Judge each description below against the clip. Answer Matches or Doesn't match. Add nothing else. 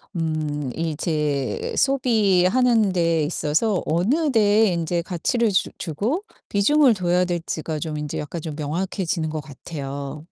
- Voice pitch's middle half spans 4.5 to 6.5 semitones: Matches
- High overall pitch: Doesn't match